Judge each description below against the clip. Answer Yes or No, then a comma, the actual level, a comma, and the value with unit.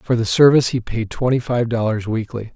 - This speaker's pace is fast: Yes, fast, 210 wpm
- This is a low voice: Yes, low, 120 Hz